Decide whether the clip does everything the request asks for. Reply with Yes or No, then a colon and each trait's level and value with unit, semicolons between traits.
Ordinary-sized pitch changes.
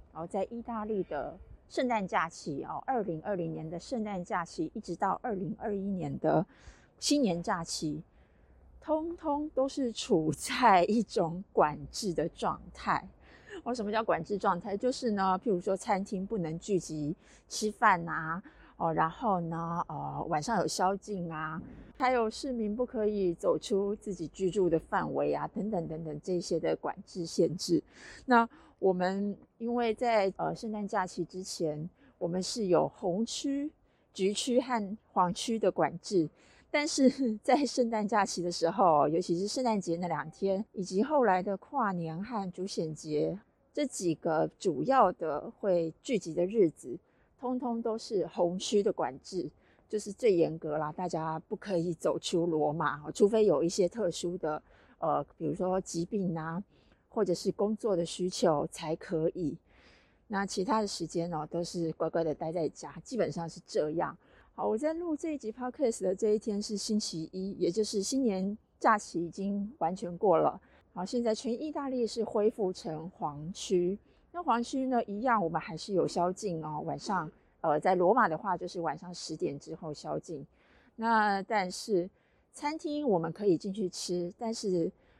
Yes: average, 4.8 semitones